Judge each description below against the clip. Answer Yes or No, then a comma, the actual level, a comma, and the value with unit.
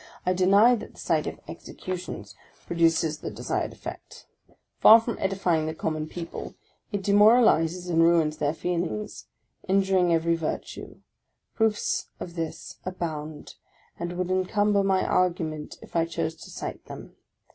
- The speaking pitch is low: No, medium, 175 Hz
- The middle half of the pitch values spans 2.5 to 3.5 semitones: Yes, average, 3.0 semitones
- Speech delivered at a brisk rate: No, average, 140 wpm